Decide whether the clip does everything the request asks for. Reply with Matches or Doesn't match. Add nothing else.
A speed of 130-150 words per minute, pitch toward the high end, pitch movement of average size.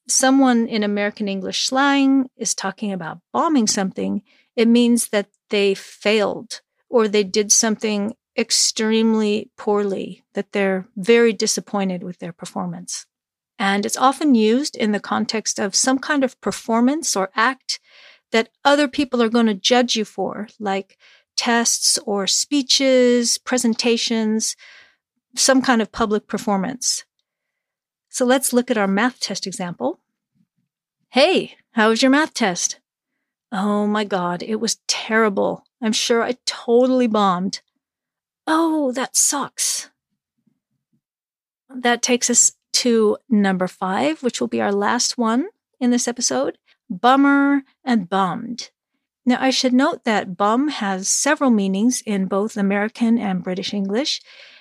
Matches